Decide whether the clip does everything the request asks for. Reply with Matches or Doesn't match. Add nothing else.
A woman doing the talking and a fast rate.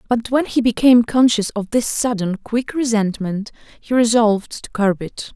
Doesn't match